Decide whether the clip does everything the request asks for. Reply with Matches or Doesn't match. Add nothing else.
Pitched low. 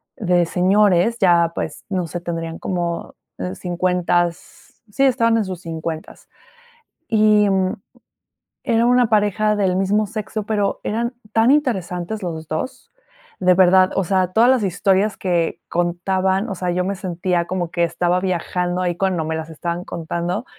Doesn't match